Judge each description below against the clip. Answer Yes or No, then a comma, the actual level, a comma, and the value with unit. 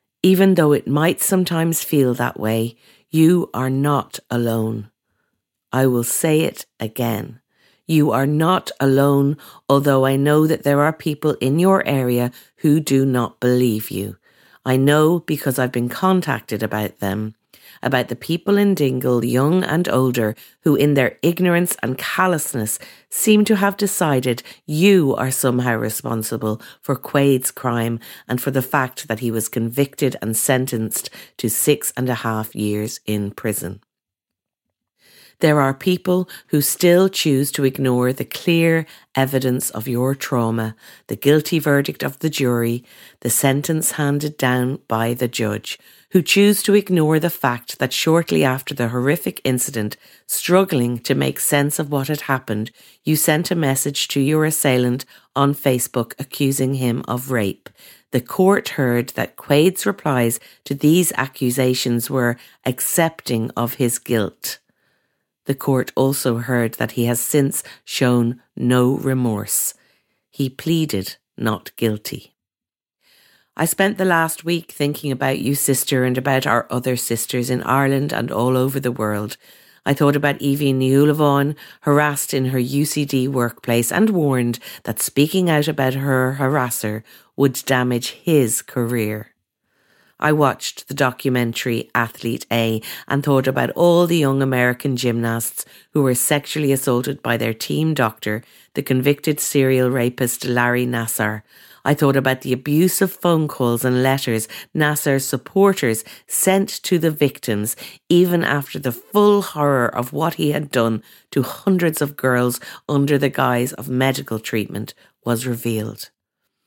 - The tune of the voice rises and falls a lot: No, average, 3.8 semitones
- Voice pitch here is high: No, low, 135 Hz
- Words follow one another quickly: No, average, 145 wpm